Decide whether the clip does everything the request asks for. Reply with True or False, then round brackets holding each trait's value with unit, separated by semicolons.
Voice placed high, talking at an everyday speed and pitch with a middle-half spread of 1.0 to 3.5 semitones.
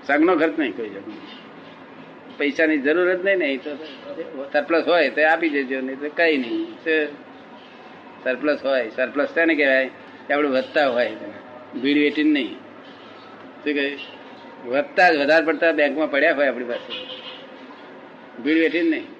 False (150 Hz; 115 wpm; 2.9 semitones)